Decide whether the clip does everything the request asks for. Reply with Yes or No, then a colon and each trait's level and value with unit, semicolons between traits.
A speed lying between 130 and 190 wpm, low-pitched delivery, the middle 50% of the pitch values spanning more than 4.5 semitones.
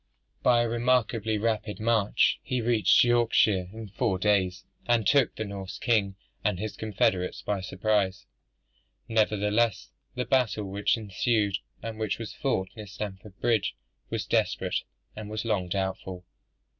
No: average, 140 wpm; low, 105 Hz; average, 2.9 semitones